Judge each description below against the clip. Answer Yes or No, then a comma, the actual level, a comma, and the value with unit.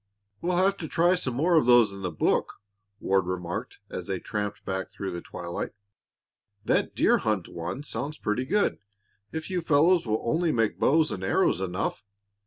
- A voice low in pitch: Yes, low, 115 Hz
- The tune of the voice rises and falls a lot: Yes, wide, 9.0 semitones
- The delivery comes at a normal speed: Yes, average, 180 wpm